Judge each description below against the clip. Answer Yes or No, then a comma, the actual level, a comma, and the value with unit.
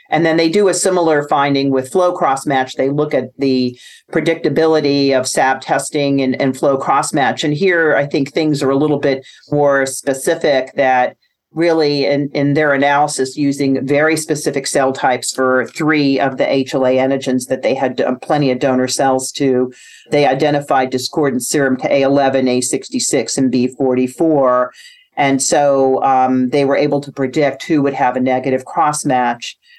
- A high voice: No, medium, 140 Hz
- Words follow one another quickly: No, average, 170 wpm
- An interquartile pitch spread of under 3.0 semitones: Yes, narrow, 2.5 semitones